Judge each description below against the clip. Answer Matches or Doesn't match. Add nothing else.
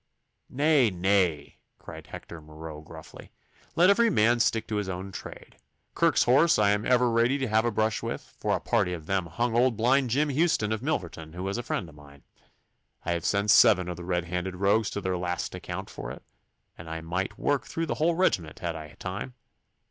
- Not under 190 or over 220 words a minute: Matches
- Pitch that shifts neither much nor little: Doesn't match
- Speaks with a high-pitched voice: Doesn't match